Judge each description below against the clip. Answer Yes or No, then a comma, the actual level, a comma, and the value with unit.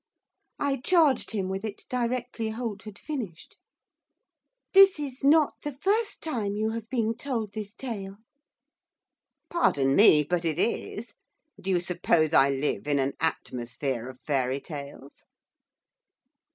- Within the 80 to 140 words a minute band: Yes, slow, 135 wpm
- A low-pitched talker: No, high, 210 Hz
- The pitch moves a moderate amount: No, wide, 8.5 semitones